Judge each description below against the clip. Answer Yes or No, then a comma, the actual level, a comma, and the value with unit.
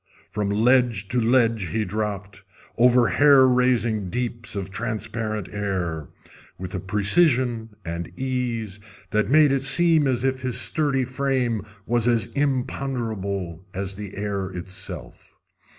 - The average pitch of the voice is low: Yes, low, 115 Hz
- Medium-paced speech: No, slow, 130 wpm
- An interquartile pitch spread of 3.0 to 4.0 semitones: No, average, 4.4 semitones